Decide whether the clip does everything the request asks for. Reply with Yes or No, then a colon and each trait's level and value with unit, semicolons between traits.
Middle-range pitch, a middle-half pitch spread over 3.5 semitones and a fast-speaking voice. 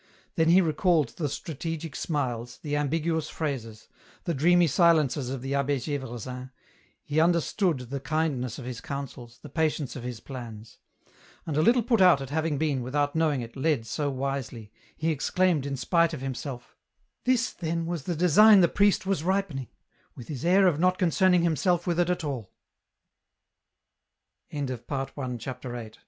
No: medium, 150 Hz; average, 4.5 semitones; average, 160 wpm